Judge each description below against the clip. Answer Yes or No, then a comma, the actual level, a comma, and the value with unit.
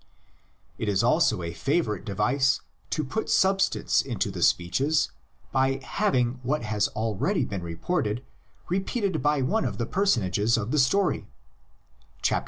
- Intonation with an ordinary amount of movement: No, wide, 6.7 semitones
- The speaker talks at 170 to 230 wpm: No, average, 140 wpm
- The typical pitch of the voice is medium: No, low, 130 Hz